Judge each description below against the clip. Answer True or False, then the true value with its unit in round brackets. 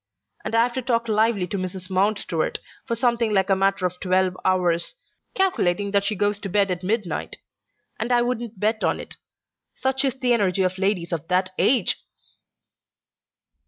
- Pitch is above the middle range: True (200 Hz)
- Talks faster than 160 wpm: True (170 wpm)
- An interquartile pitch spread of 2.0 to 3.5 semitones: False (4.0 semitones)